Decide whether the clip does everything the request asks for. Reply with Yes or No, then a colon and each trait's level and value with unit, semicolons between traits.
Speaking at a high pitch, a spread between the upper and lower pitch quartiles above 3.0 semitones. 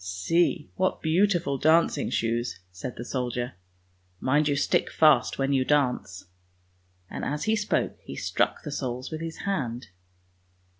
No: low, 135 Hz; average, 5.0 semitones